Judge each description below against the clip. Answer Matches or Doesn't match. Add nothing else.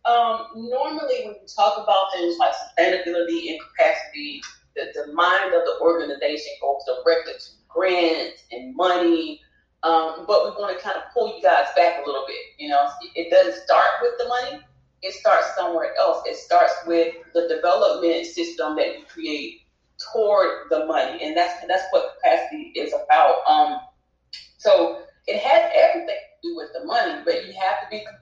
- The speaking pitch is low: Doesn't match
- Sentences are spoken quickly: Doesn't match